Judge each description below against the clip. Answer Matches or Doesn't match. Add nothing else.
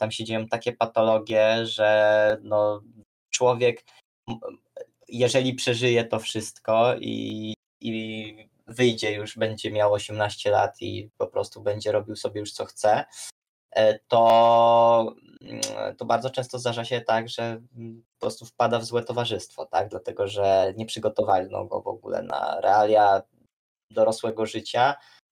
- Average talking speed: Matches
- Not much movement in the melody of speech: Matches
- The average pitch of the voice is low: Matches